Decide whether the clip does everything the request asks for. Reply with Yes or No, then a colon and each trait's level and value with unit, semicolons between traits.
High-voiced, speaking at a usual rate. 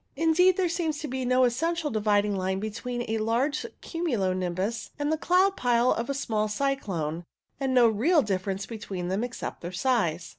Yes: high, 235 Hz; average, 180 wpm